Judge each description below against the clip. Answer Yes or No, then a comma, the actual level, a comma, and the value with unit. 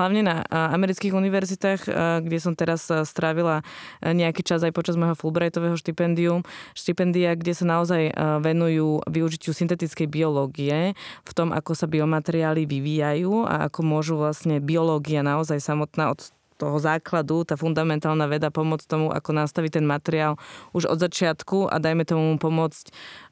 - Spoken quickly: No, average, 140 wpm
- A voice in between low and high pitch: Yes, medium, 160 Hz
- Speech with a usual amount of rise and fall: No, narrow, 1.7 semitones